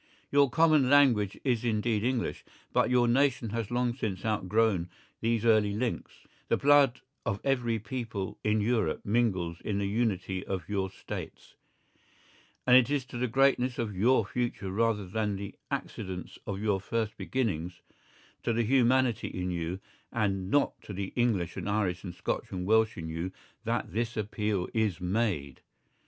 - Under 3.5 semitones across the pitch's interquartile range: No, average, 3.9 semitones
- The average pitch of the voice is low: Yes, low, 110 Hz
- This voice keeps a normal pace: Yes, average, 160 wpm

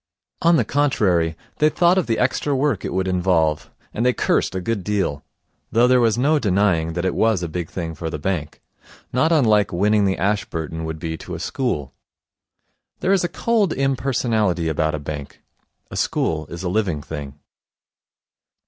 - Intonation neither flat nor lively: No, wide, 7.5 semitones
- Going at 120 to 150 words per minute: No, average, 180 wpm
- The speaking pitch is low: Yes, very low, 95 Hz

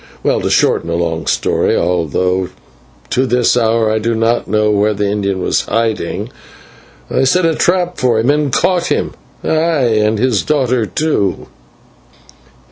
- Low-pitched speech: Yes, low, 115 Hz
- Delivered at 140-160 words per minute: Yes, average, 155 wpm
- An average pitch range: Yes, average, 4.7 semitones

